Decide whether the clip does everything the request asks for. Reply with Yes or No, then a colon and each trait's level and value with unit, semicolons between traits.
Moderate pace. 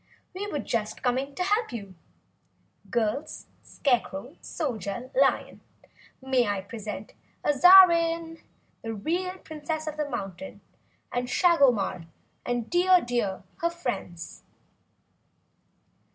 No: slow, 105 wpm